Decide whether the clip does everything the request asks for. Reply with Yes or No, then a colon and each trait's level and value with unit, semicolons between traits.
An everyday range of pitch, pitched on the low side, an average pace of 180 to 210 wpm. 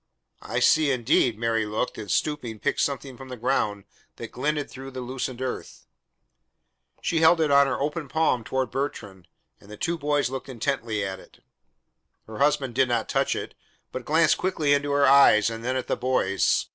Yes: average, 3.8 semitones; low, 130 Hz; average, 185 wpm